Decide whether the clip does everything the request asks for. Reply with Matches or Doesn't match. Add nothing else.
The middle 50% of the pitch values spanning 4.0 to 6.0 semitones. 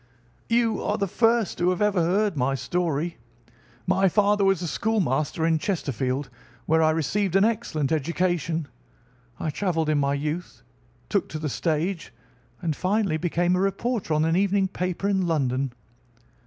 Matches